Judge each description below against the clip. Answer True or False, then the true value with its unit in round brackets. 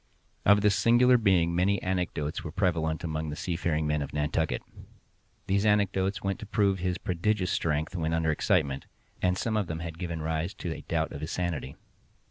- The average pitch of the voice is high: False (85 Hz)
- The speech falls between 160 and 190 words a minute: True (185 wpm)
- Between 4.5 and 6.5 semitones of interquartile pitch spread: False (3.6 semitones)